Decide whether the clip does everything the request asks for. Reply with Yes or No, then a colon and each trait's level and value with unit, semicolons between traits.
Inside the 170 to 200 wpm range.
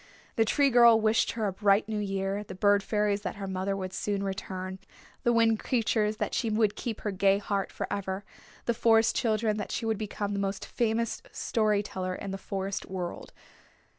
Yes: average, 195 wpm